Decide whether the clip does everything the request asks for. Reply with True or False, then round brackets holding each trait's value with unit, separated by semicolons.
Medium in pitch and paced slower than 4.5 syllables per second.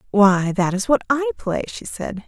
False (210 Hz; 4.3 syllables/s)